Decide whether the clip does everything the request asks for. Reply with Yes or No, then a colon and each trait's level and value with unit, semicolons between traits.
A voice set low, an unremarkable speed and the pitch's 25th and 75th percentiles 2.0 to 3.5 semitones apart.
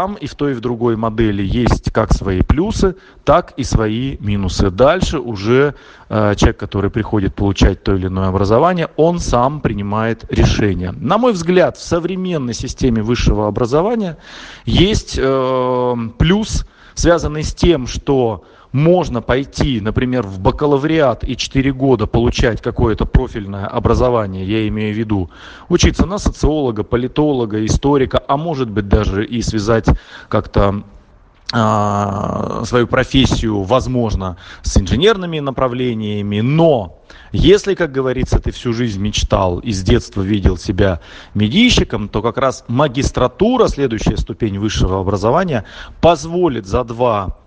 No: low, 115 Hz; average, 130 wpm; average, 4.3 semitones